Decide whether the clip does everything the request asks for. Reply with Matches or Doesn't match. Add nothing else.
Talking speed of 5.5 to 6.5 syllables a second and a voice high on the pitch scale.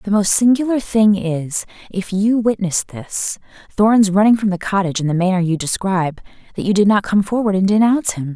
Matches